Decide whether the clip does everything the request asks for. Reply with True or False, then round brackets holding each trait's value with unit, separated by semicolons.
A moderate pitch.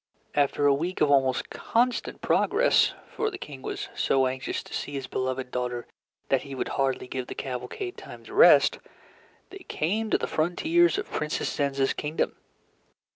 True (145 Hz)